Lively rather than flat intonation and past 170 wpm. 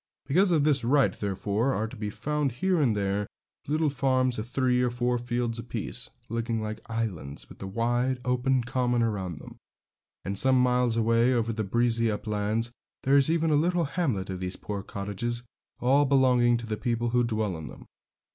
No: average, 3.3 semitones; average, 190 wpm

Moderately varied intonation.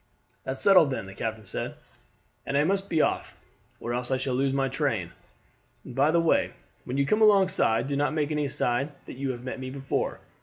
Yes: average, 3.3 semitones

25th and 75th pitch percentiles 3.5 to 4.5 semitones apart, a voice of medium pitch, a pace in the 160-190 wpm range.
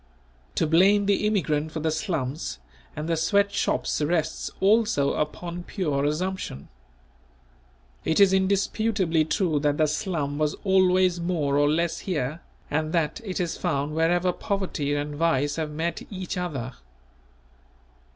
No: average, 3.9 semitones; medium, 165 Hz; average, 140 wpm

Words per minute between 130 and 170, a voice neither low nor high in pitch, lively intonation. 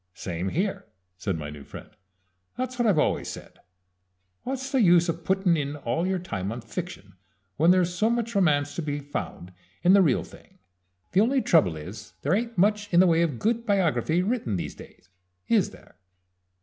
No: average, 190 wpm; medium, 175 Hz; wide, 7.4 semitones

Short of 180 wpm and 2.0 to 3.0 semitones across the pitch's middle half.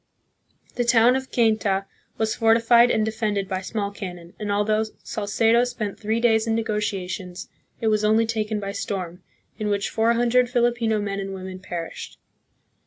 Yes: average, 160 wpm; narrow, 2.4 semitones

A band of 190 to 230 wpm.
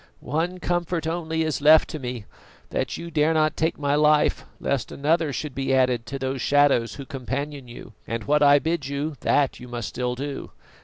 Yes: average, 195 wpm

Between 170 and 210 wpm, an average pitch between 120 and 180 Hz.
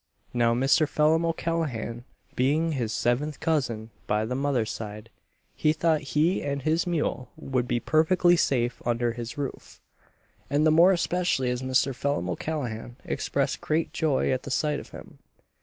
No: average, 155 wpm; medium, 140 Hz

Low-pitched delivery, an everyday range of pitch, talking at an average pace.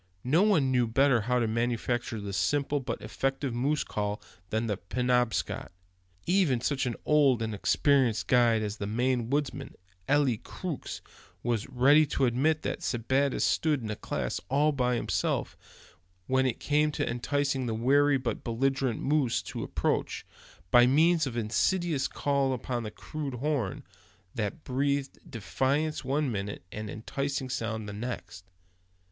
Yes: low, 130 Hz; average, 3.6 semitones; average, 150 wpm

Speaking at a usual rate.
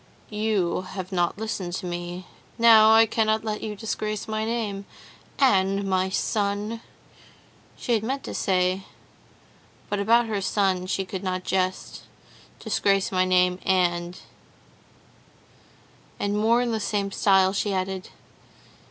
No: slow, 125 wpm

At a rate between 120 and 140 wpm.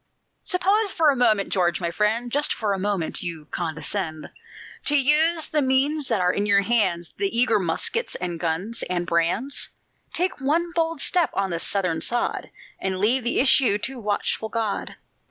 No: average, 175 wpm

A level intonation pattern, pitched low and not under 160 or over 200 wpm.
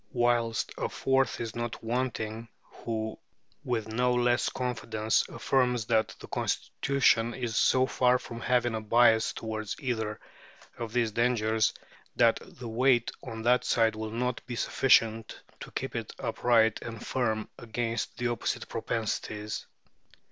No: narrow, 1.7 semitones; low, 115 Hz; average, 140 wpm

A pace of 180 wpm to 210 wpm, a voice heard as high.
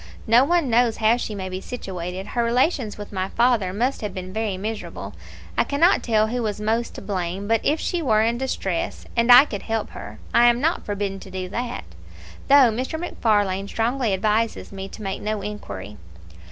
Yes: average, 195 wpm; high, 220 Hz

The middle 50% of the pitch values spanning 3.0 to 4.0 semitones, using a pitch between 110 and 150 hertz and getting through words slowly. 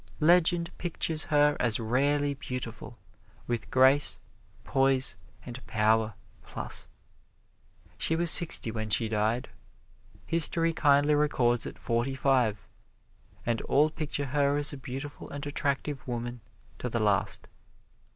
Yes: average, 3.6 semitones; low, 135 Hz; slow, 120 wpm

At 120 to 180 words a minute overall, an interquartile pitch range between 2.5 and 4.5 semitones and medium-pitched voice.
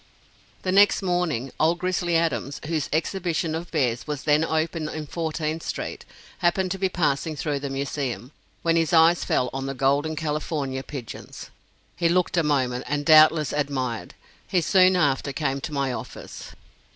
Yes: average, 165 wpm; average, 3.5 semitones; medium, 155 Hz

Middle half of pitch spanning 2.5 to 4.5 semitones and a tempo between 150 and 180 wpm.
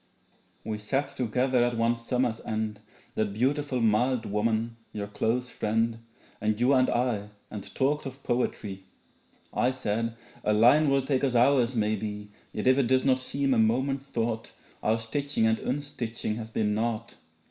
Yes: average, 3.1 semitones; average, 160 wpm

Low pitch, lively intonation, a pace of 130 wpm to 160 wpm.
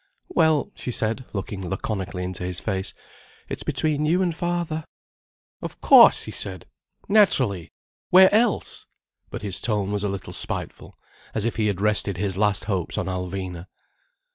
Yes: low, 105 Hz; wide, 8.2 semitones; average, 155 wpm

